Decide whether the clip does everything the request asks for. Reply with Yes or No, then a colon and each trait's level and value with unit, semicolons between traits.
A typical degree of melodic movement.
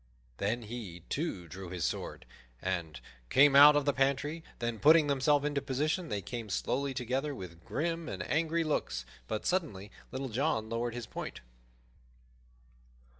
No: wide, 5.9 semitones